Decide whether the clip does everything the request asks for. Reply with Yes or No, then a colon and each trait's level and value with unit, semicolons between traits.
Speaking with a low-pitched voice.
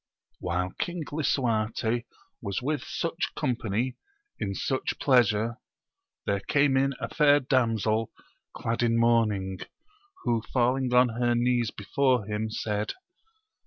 Yes: low, 120 Hz